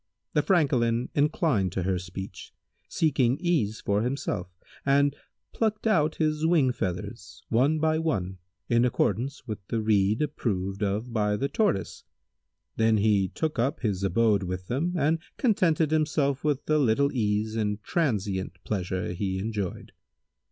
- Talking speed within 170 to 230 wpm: No, average, 145 wpm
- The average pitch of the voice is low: Yes, low, 115 Hz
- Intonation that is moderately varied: No, wide, 7.0 semitones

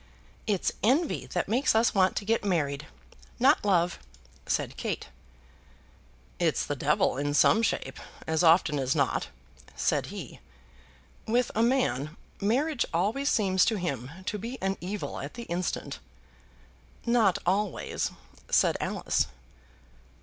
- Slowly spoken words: Yes, slow, 130 wpm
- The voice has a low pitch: No, high, 195 Hz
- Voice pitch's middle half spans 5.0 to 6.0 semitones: Yes, average, 5.3 semitones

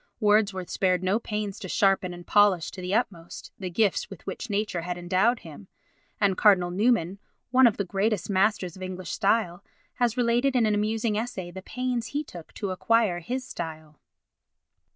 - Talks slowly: No, average, 175 wpm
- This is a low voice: No, high, 200 Hz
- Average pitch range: Yes, average, 3.7 semitones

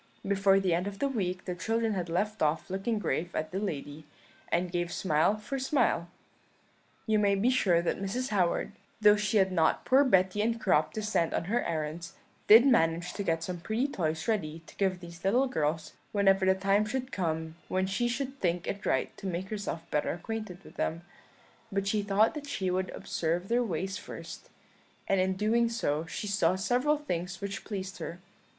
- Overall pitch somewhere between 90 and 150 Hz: No, high, 195 Hz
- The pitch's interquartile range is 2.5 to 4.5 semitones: Yes, average, 4.1 semitones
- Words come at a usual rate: Yes, average, 195 wpm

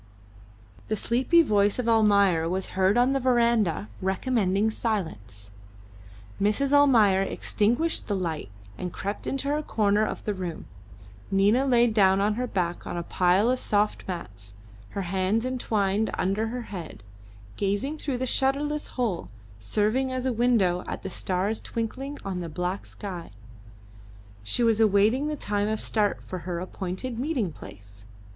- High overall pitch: Yes, high, 205 Hz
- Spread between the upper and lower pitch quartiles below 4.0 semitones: No, average, 4.7 semitones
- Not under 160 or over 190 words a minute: No, average, 150 wpm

